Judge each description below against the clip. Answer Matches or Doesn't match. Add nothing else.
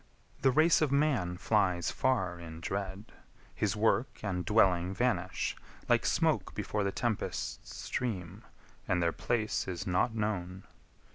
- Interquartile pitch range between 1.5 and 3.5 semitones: Doesn't match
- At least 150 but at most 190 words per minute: Doesn't match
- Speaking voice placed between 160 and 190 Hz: Doesn't match